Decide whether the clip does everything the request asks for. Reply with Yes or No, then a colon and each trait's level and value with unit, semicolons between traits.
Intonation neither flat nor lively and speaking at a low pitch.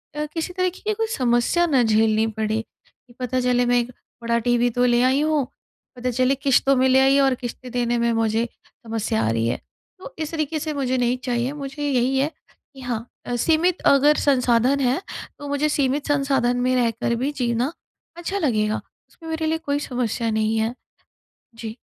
No: average, 3.4 semitones; very high, 255 Hz